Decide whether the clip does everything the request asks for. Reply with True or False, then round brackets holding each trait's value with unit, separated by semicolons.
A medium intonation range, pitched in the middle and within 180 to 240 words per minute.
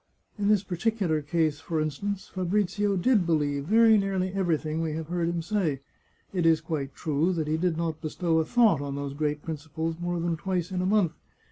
True (3.5 semitones; 170 Hz; 200 wpm)